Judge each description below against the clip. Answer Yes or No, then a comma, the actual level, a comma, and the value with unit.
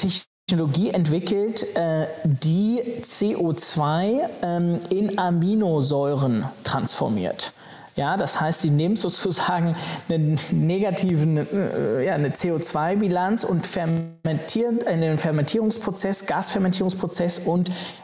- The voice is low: No, medium, 175 Hz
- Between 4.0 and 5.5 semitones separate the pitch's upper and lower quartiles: No, average, 3.6 semitones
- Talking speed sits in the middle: No, slow, 90 wpm